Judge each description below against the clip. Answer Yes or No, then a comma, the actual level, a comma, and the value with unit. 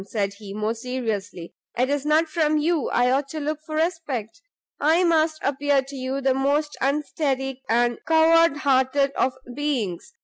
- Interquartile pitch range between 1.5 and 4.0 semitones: Yes, average, 3.6 semitones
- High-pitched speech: Yes, very high, 275 Hz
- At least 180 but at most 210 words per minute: No, average, 165 wpm